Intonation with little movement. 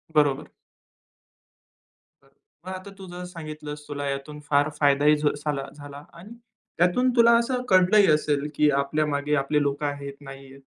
No: average, 3.7 semitones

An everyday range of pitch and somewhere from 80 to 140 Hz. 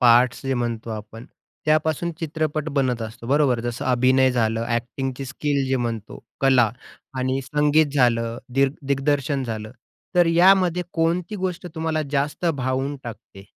Yes: average, 4.2 semitones; low, 135 Hz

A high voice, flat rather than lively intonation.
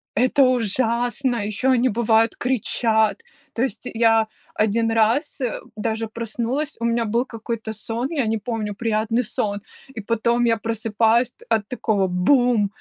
Yes: high, 230 Hz; narrow, 1.9 semitones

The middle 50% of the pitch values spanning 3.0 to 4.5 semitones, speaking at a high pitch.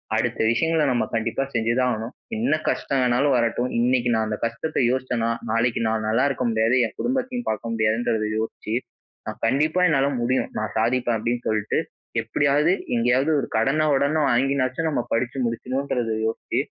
No: average, 3.3 semitones; low, 125 Hz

